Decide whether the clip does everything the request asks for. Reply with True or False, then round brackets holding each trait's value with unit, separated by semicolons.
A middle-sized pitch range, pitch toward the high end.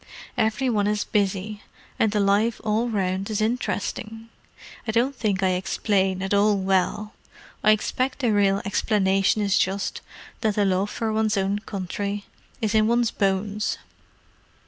False (2.0 semitones; 205 Hz)